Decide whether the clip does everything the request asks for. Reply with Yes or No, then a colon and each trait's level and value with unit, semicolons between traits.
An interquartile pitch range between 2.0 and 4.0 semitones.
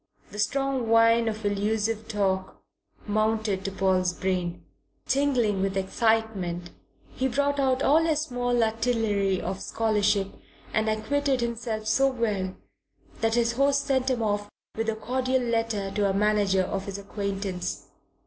Yes: average, 3.6 semitones